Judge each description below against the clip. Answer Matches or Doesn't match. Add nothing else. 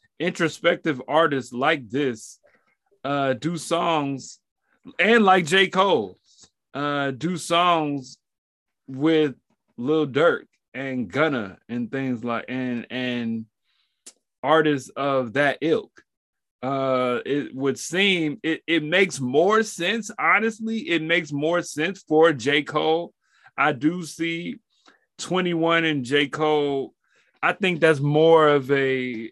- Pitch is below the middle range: Doesn't match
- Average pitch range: Matches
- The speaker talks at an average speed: Doesn't match